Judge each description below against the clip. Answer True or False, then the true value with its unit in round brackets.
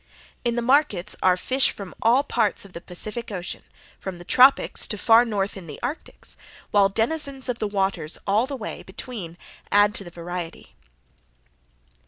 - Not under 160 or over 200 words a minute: True (170 wpm)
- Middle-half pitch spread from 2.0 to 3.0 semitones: False (4.7 semitones)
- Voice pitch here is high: True (210 Hz)